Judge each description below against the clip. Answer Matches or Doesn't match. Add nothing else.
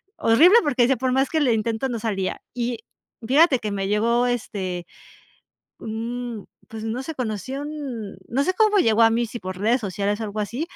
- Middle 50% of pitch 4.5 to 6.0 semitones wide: Doesn't match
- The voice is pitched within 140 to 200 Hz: Doesn't match